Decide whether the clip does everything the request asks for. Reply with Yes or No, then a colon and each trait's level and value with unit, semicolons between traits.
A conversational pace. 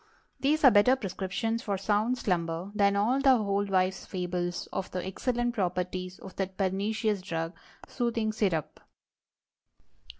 No: slow, 130 wpm